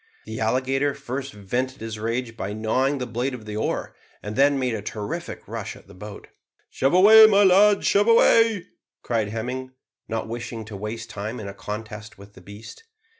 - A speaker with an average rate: Yes, average, 185 wpm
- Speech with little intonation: No, average, 4.2 semitones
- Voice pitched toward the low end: Yes, low, 115 Hz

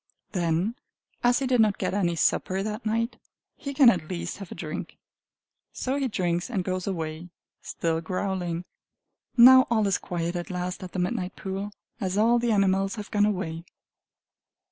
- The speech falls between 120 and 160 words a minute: No, average, 170 wpm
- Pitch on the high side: Yes, high, 195 Hz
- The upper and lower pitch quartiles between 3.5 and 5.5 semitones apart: Yes, average, 3.9 semitones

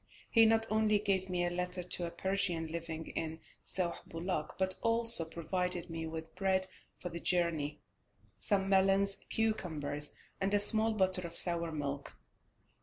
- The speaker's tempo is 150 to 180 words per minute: Yes, average, 155 wpm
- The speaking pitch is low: No, medium, 180 Hz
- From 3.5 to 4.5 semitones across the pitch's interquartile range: No, average, 3.1 semitones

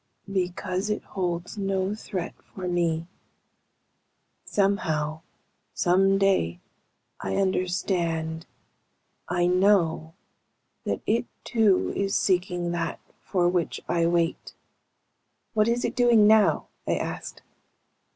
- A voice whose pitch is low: No, medium, 180 Hz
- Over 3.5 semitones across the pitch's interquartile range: No, average, 2.7 semitones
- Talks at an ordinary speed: No, slow, 100 wpm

